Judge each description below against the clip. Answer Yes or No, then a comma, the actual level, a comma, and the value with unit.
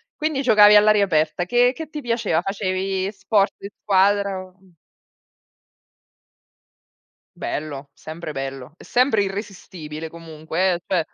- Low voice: No, high, 190 Hz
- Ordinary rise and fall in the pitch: Yes, average, 4.2 semitones